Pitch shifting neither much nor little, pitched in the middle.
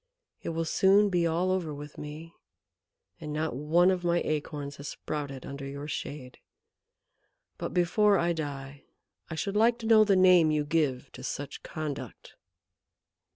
Yes: average, 3.7 semitones; medium, 155 Hz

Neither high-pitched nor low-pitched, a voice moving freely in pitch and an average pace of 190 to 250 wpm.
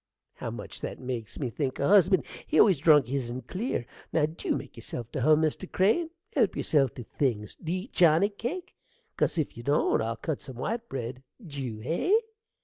Yes: medium, 150 Hz; wide, 6.8 semitones; average, 195 wpm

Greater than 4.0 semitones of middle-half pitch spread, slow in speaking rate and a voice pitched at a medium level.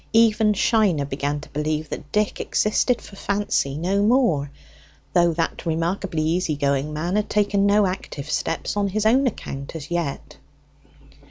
No: wide, 5.5 semitones; average, 155 wpm; medium, 175 Hz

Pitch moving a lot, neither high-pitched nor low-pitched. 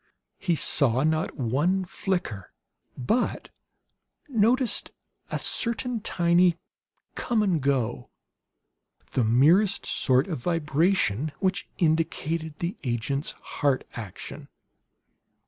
Yes: wide, 6.3 semitones; medium, 160 Hz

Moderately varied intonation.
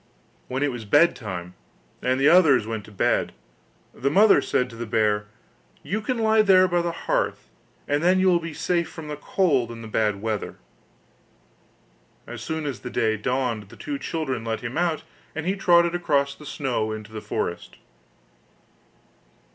No: wide, 7.4 semitones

